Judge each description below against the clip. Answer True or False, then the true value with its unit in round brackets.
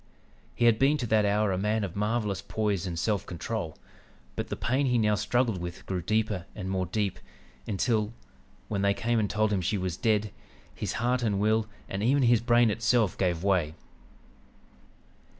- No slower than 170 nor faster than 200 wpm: True (185 wpm)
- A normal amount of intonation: True (3.1 semitones)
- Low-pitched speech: True (105 Hz)